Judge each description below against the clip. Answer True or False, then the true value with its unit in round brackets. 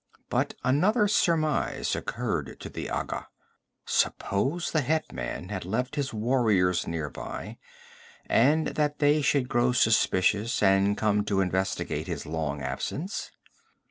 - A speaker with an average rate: False (125 wpm)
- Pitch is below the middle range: True (115 Hz)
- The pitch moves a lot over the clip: True (7.6 semitones)